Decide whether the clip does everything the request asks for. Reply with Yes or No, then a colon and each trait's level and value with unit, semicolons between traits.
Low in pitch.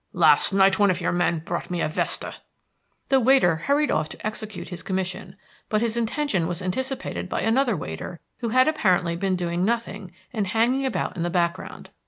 No: high, 195 Hz